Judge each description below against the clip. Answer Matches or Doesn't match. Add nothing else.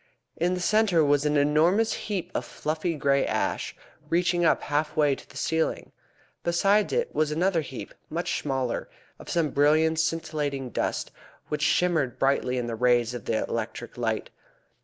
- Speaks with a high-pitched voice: Doesn't match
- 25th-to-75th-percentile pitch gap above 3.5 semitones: Matches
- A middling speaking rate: Matches